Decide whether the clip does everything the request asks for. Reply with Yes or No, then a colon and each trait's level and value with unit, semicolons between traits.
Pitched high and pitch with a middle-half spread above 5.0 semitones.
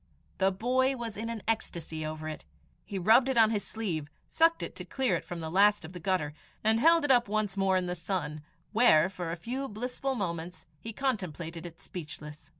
Yes: high, 195 Hz; wide, 5.6 semitones